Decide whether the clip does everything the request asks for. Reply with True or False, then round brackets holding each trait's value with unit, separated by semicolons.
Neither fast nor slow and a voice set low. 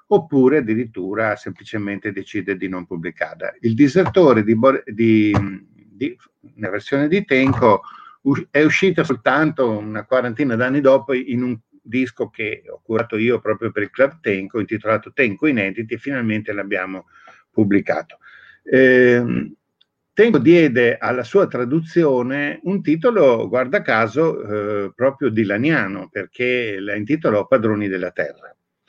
True (130 wpm; 125 Hz)